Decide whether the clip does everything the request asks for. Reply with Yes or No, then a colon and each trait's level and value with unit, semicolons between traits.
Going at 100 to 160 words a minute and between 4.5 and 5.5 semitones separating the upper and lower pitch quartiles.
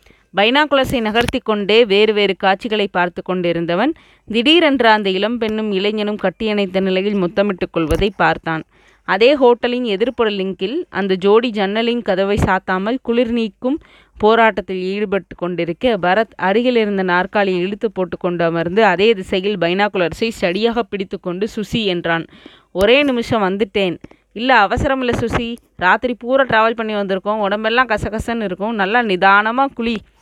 No: average, 125 wpm; average, 3.5 semitones